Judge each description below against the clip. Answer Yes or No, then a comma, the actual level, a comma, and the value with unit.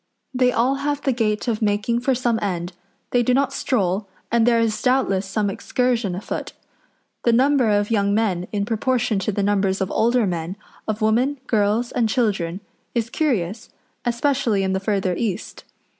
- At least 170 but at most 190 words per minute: Yes, average, 175 wpm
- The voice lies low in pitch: No, high, 220 Hz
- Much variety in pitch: No, average, 3.6 semitones